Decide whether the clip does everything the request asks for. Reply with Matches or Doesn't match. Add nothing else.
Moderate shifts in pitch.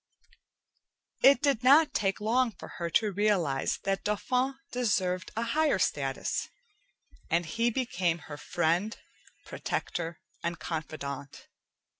Doesn't match